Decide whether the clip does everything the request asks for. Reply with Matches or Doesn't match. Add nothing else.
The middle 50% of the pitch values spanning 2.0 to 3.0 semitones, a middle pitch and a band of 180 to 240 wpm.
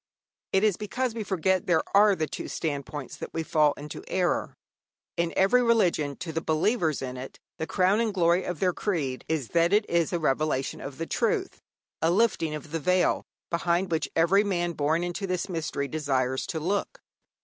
Doesn't match